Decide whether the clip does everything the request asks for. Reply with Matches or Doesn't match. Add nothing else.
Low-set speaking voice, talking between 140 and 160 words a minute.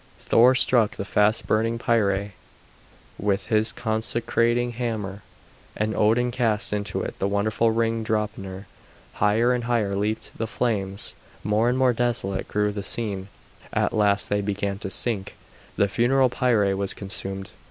Matches